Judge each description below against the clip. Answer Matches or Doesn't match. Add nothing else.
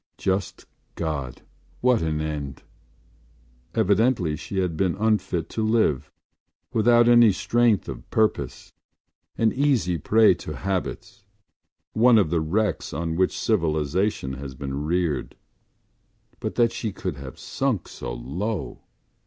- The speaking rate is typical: Doesn't match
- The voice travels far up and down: Matches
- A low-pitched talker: Matches